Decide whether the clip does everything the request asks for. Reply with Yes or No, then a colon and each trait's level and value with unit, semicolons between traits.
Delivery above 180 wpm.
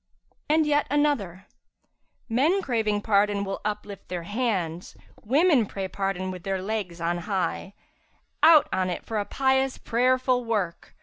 No: average, 145 wpm